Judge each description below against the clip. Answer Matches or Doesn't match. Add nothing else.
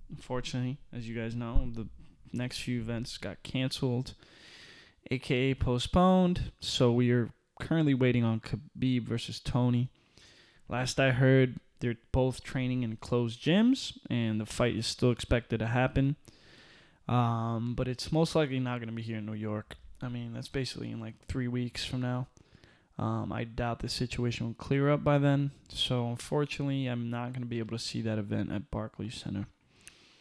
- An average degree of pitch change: Doesn't match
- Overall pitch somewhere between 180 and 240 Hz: Doesn't match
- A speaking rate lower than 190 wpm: Matches